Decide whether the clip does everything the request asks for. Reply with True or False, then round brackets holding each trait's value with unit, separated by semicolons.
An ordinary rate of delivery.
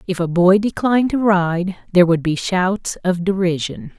True (180 wpm)